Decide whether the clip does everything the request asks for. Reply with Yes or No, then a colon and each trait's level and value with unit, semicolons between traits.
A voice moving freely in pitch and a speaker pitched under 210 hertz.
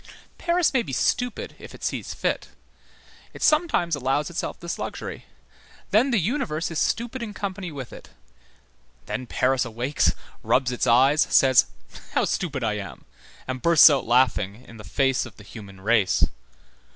Yes: wide, 7.5 semitones; low, 135 Hz